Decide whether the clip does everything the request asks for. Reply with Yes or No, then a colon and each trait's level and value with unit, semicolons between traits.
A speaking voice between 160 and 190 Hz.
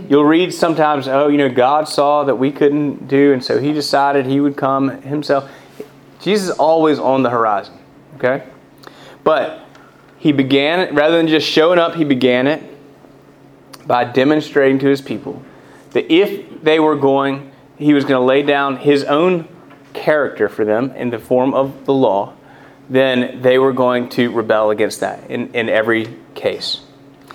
No: medium, 140 Hz